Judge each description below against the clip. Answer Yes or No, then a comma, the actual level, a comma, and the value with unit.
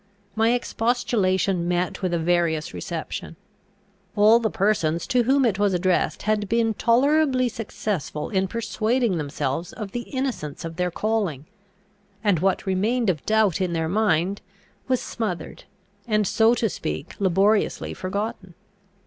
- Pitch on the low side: No, high, 200 Hz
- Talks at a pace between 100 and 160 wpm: Yes, average, 140 wpm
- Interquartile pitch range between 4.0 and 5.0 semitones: Yes, average, 4.3 semitones